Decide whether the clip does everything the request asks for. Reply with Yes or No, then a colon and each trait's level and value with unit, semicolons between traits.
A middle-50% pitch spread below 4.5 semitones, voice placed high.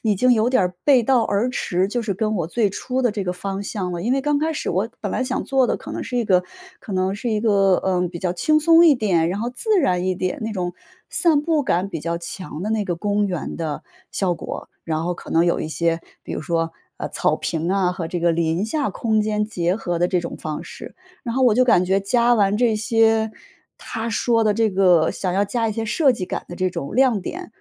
No: average, 4.8 semitones; high, 205 Hz